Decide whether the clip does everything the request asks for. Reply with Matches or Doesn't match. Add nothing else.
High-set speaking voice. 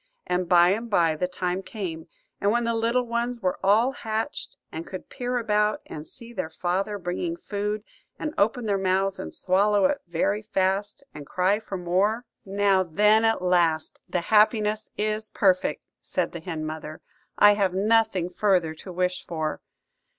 Matches